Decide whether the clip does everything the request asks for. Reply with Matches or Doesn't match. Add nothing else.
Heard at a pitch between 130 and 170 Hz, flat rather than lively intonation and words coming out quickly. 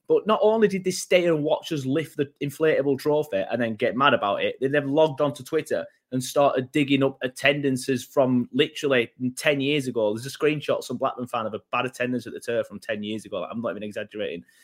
Doesn't match